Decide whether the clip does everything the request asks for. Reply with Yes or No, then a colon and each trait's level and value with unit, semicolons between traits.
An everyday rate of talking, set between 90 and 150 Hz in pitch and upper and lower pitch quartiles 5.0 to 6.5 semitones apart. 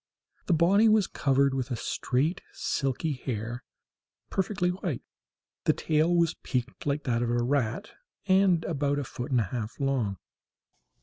Yes: average, 150 wpm; medium, 140 Hz; wide, 5.6 semitones